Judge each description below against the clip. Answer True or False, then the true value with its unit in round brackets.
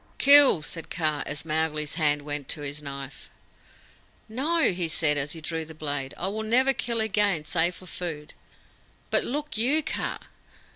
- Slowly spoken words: False (165 wpm)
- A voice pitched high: False (160 Hz)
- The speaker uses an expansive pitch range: True (6.7 semitones)